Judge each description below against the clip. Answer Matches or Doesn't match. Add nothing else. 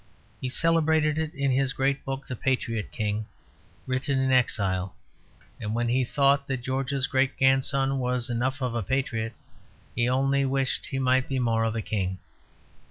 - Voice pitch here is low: Matches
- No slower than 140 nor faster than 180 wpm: Matches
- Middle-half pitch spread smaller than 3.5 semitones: Matches